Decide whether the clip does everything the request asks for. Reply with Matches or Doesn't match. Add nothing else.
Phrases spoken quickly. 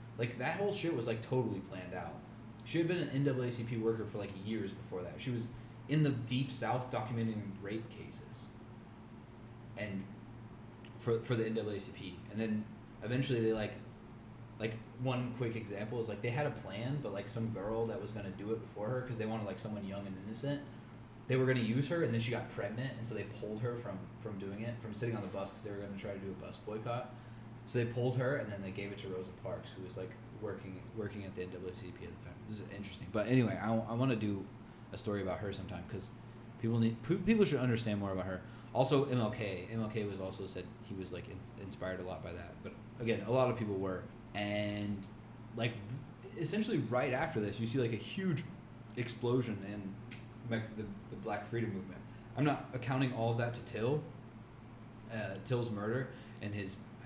Matches